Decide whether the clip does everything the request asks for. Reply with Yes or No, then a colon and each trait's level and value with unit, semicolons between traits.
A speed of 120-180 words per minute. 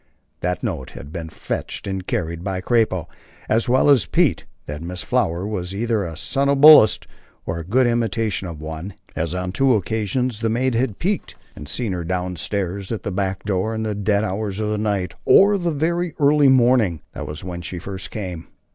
No: average, 195 wpm